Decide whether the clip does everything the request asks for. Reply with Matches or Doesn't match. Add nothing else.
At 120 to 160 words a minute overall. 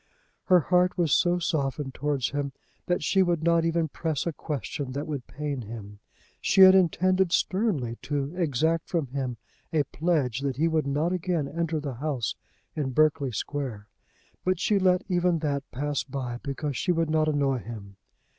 Doesn't match